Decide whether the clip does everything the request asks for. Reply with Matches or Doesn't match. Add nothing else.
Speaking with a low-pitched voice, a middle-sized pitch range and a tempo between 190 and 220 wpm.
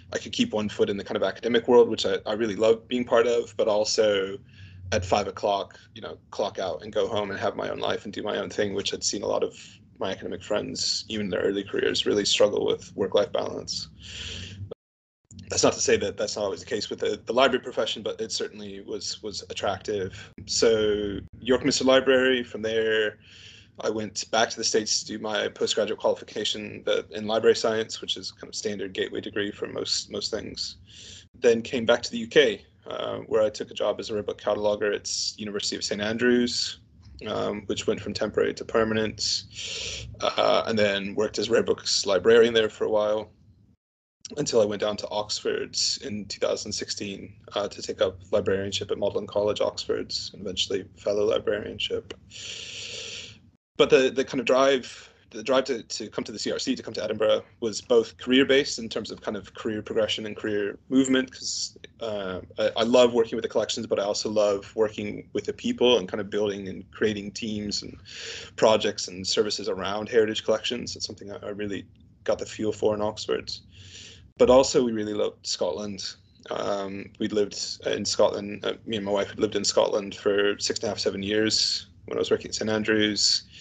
Doesn't match